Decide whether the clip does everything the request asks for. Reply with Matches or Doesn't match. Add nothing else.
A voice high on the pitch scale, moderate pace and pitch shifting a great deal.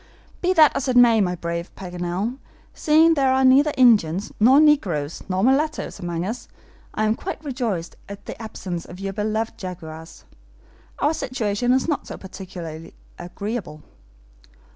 Matches